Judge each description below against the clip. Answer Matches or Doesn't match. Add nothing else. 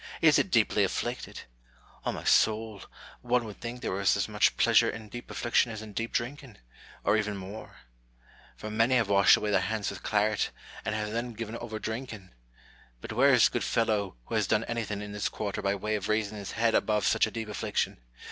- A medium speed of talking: Doesn't match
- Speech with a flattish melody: Matches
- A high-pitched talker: Doesn't match